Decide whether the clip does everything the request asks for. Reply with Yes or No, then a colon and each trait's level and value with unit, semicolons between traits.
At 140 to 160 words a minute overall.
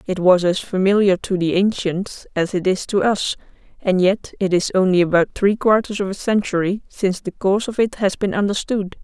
No: fast, 205 wpm